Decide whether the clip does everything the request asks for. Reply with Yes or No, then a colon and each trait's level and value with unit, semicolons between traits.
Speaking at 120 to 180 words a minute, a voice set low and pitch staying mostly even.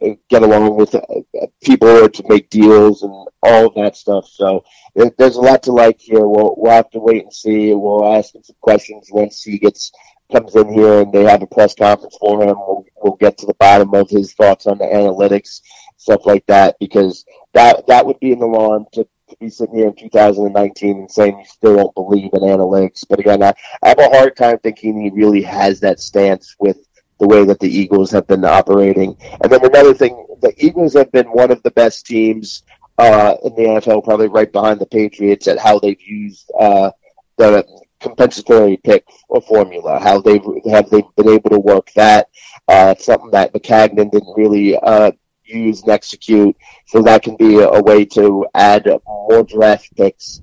No: average, 200 wpm; low, 105 Hz; narrow, 2.0 semitones